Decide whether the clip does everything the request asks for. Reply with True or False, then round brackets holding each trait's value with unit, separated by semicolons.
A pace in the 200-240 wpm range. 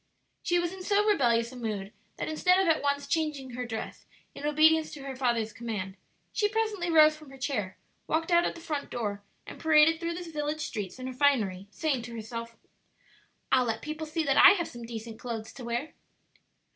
True (205 wpm)